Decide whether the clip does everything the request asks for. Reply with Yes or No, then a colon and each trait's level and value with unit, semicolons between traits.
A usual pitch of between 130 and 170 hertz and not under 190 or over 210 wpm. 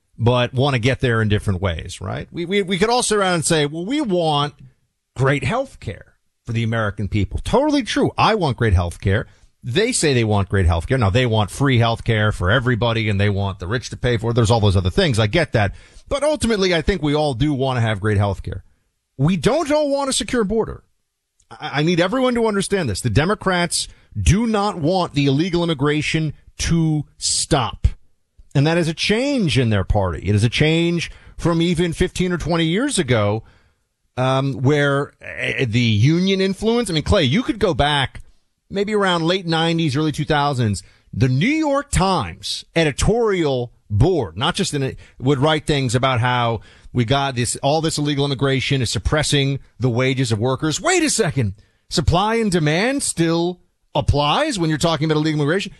Yes: medium, 140 Hz; average, 200 wpm